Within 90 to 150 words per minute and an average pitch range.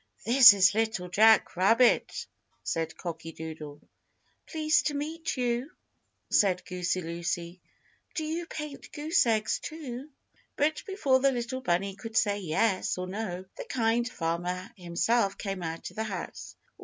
No: average, 145 wpm; wide, 6.4 semitones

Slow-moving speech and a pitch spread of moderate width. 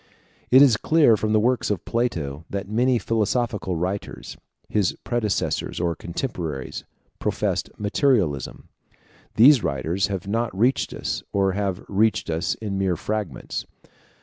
Yes: slow, 130 wpm; average, 4.4 semitones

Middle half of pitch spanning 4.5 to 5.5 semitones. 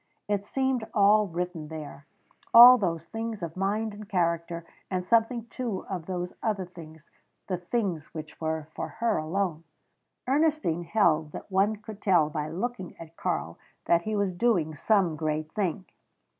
Yes: average, 4.8 semitones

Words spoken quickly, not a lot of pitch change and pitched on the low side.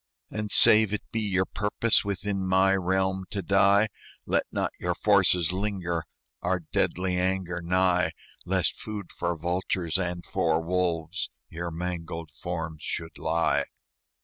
No: slow, 135 wpm; narrow, 2.3 semitones; very low, 90 Hz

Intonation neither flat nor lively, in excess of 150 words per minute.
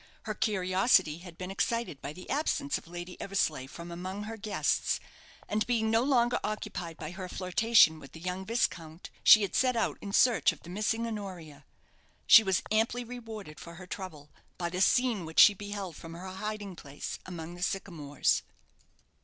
Yes: average, 4.3 semitones; average, 180 wpm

